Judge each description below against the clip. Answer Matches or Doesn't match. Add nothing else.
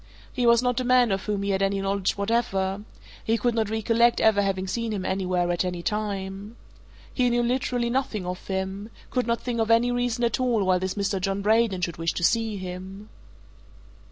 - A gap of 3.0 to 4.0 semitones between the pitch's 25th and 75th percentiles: Matches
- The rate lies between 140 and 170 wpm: Doesn't match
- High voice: Matches